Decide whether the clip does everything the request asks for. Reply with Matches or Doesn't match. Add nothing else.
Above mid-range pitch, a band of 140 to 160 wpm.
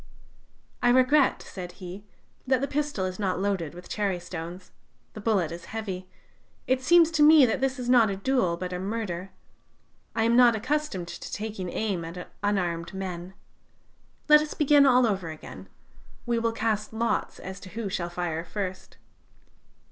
Doesn't match